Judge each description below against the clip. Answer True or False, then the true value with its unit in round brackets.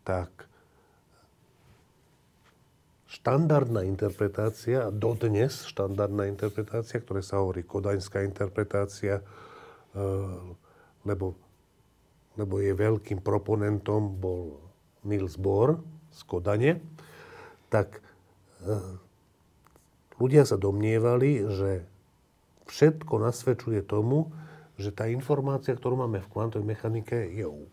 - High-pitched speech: False (105 Hz)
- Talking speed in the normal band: False (85 wpm)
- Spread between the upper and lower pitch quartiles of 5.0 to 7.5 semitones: False (3.5 semitones)